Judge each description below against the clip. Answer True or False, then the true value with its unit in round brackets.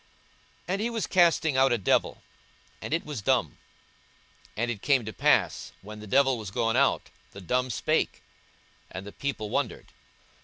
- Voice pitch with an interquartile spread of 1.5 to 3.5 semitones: False (4.8 semitones)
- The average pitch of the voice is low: True (125 Hz)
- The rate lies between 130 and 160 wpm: False (170 wpm)